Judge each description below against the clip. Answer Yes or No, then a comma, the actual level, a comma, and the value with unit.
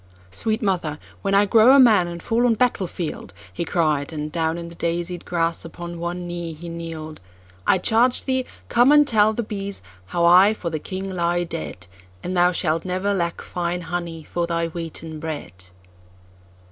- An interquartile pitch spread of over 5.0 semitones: No, average, 3.3 semitones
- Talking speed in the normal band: Yes, average, 170 wpm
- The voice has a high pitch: No, medium, 175 Hz